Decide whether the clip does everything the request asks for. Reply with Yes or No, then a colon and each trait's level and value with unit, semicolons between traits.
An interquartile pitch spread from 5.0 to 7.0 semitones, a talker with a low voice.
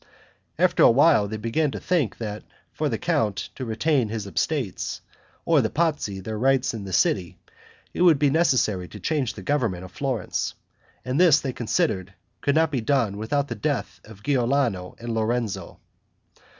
Yes: wide, 5.4 semitones; low, 120 Hz